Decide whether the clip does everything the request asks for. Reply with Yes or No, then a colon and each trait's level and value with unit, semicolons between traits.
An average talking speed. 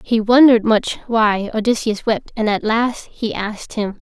Yes: average, 175 wpm